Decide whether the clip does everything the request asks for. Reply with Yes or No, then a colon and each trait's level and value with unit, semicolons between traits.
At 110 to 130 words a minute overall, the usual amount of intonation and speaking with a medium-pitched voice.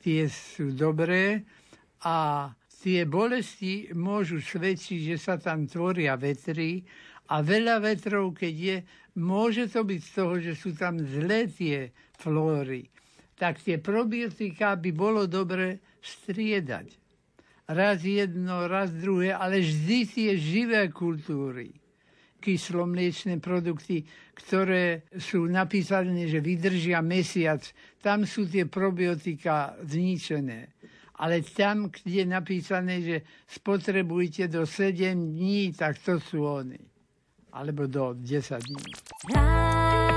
Yes: average, 115 wpm; average, 3.6 semitones; medium, 180 Hz